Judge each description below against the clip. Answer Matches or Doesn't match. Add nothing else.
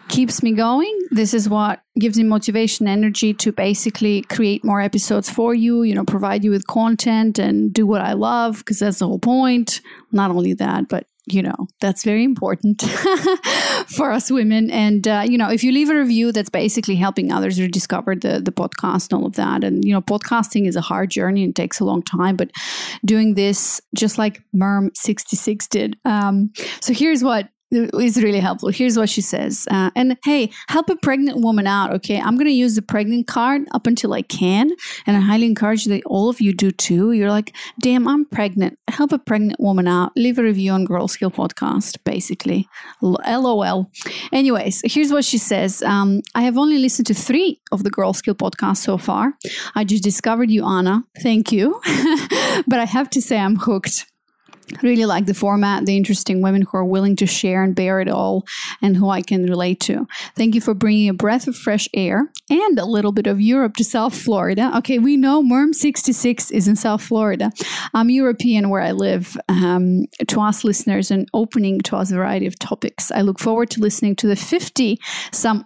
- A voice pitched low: Doesn't match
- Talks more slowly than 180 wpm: Doesn't match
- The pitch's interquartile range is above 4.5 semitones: Doesn't match